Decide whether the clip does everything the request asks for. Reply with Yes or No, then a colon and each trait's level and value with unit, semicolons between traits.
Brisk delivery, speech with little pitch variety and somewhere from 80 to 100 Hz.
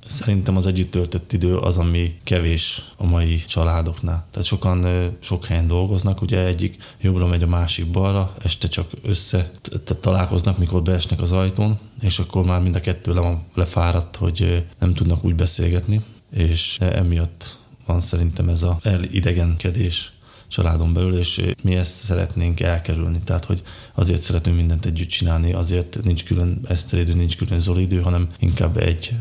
Yes: fast, 160 wpm; narrow, 2.1 semitones; very low, 90 Hz